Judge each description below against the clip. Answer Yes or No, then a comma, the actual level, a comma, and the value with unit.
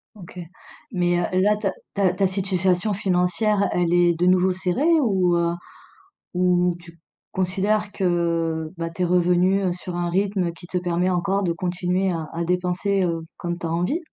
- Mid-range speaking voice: Yes, medium, 180 Hz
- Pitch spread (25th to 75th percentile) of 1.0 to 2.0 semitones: Yes, narrow, 1.7 semitones